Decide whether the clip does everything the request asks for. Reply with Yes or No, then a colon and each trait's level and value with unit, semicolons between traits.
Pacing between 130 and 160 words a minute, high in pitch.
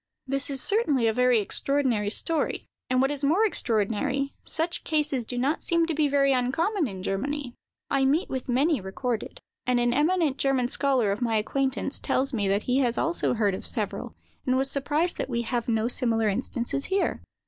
No: average, 190 wpm; very high, 265 Hz